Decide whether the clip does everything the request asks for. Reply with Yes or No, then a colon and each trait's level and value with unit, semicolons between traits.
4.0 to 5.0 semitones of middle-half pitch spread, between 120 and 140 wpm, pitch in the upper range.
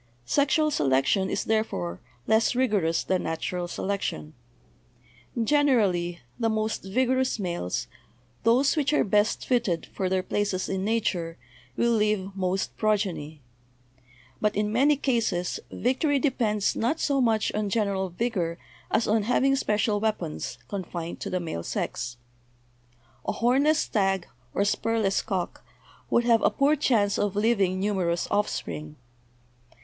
Yes: average, 4.4 semitones; slow, 135 wpm; high, 210 Hz